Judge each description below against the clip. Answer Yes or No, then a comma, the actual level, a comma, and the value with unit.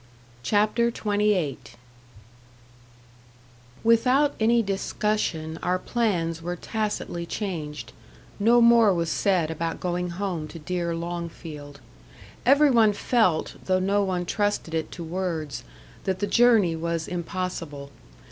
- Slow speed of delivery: Yes, slow, 115 wpm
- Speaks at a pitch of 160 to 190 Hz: Yes, medium, 185 Hz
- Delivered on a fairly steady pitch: No, average, 4.2 semitones